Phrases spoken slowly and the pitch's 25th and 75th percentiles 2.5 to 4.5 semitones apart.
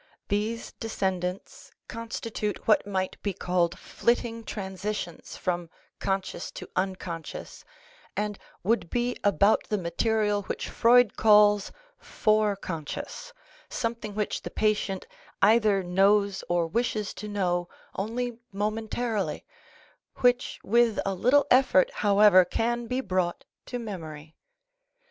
Yes: slow, 115 wpm; average, 3.3 semitones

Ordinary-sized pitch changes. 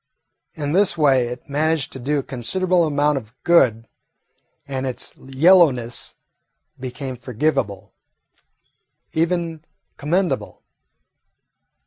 Yes: average, 4.4 semitones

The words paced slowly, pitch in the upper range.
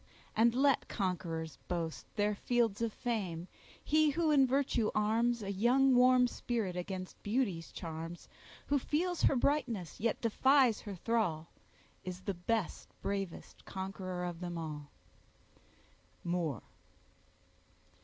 Yes: slow, 120 wpm; high, 205 Hz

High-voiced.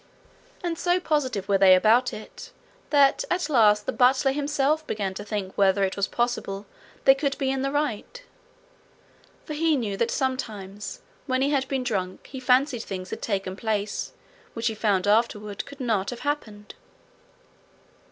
Yes: high, 235 Hz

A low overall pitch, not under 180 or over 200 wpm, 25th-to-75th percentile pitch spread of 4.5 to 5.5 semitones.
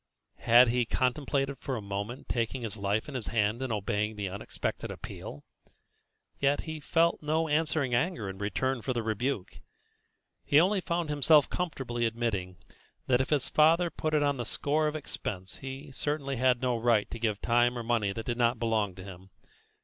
Yes: low, 120 Hz; average, 185 wpm; average, 4.8 semitones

